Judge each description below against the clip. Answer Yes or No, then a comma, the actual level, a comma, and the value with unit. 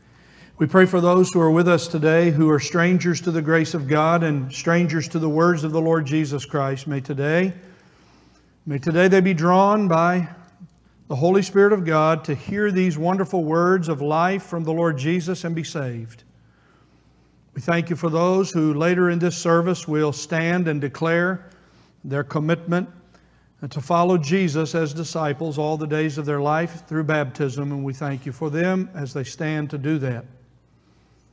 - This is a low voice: No, medium, 160 Hz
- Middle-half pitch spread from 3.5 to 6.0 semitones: No, average, 3.1 semitones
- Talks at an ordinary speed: Yes, average, 180 wpm